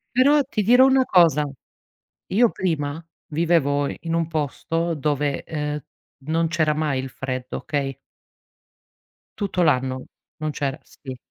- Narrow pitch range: No, average, 3.1 semitones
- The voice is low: No, medium, 155 Hz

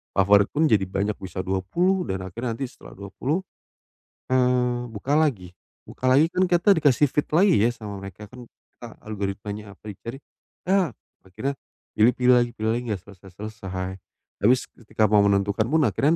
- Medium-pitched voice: No, low, 110 Hz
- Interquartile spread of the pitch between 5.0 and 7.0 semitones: Yes, average, 5.3 semitones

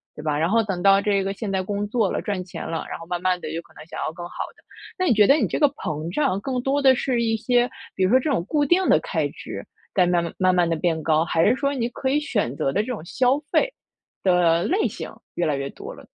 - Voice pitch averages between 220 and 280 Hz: No, high, 200 Hz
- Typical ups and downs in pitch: No, wide, 6.8 semitones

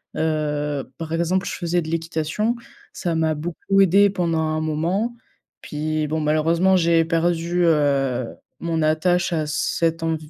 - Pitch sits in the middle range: Yes, medium, 165 Hz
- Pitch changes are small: Yes, narrow, 1.9 semitones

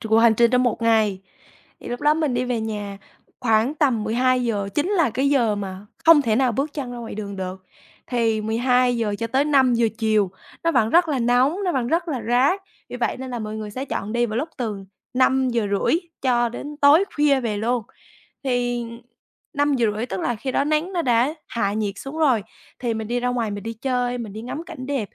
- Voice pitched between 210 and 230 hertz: No, high, 245 Hz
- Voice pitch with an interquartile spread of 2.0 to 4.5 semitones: Yes, average, 3.5 semitones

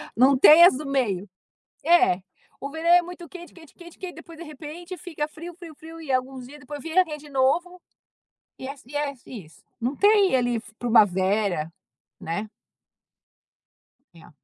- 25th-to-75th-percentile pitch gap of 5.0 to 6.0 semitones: Yes, wide, 5.6 semitones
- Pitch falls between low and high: No, very high, 295 Hz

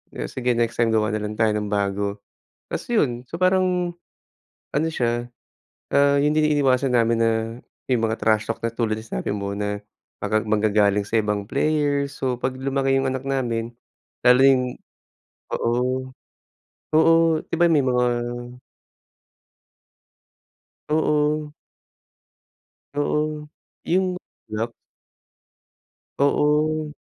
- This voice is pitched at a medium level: No, low, 130 Hz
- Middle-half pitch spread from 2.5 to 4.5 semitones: No, average, 5.2 semitones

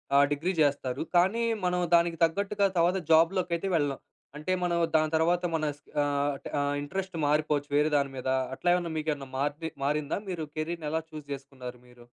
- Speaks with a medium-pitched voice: Yes, medium, 155 Hz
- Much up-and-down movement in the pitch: No, average, 3.3 semitones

